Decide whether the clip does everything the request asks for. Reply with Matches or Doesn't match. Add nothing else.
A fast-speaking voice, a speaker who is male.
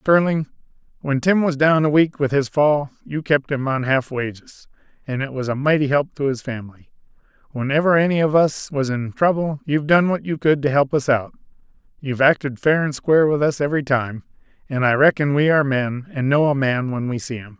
Matches